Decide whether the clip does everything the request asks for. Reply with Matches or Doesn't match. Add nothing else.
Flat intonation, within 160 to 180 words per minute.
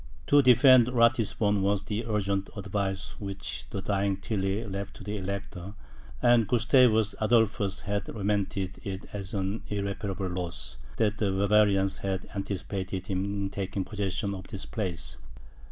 Doesn't match